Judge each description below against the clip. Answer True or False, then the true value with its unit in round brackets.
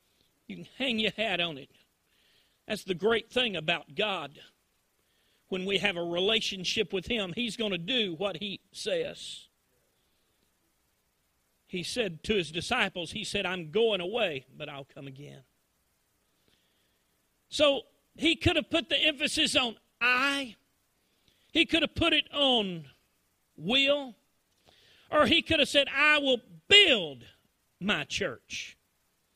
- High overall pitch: True (215 Hz)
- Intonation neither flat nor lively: False (8.1 semitones)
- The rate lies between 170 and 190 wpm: False (135 wpm)